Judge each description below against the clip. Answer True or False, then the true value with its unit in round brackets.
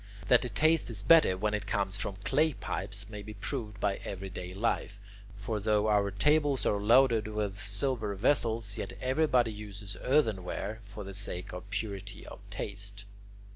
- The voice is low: True (105 Hz)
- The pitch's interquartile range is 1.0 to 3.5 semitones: True (2.7 semitones)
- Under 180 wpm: True (165 wpm)